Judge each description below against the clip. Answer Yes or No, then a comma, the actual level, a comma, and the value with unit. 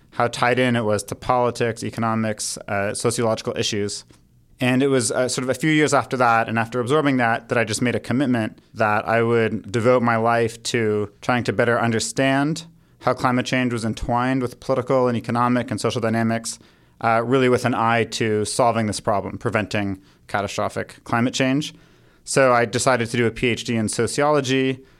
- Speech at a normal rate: Yes, average, 185 wpm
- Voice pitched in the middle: No, low, 120 Hz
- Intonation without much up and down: Yes, narrow, 2.3 semitones